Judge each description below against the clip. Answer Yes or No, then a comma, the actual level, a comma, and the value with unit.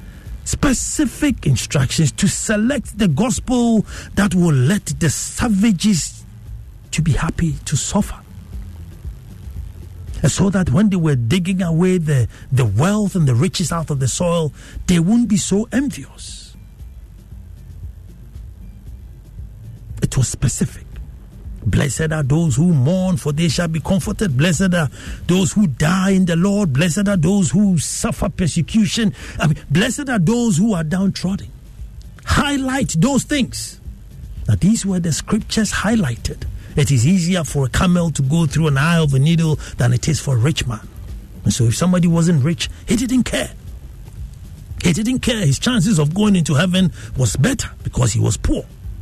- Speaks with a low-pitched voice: No, medium, 160 Hz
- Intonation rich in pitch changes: Yes, wide, 8.7 semitones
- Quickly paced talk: No, average, 155 wpm